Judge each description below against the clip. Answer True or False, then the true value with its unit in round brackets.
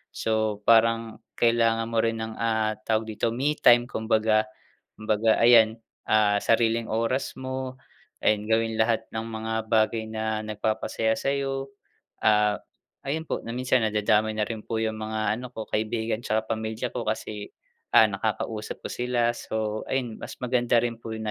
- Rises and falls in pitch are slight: True (1.3 semitones)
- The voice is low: True (110 Hz)